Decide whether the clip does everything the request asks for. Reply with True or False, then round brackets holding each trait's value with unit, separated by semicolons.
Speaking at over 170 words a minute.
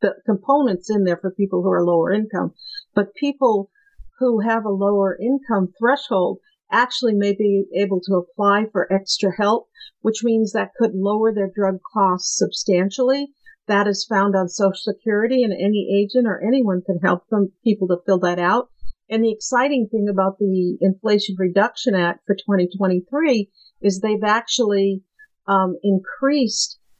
False (160 wpm)